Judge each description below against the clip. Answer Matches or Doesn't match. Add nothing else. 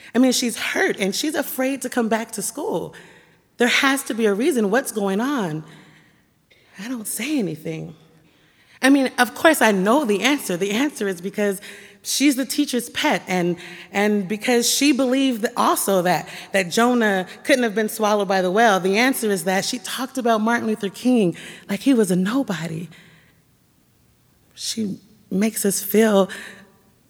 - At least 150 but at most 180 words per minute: Matches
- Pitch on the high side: Matches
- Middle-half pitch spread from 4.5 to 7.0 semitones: Matches